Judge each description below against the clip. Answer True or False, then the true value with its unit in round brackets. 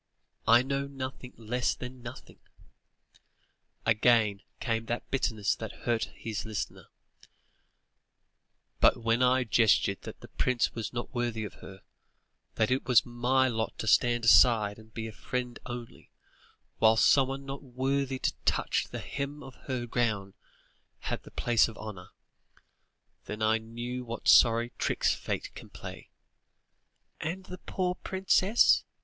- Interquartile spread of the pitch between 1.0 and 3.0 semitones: True (2.6 semitones)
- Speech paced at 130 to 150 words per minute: True (140 wpm)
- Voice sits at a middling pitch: False (120 Hz)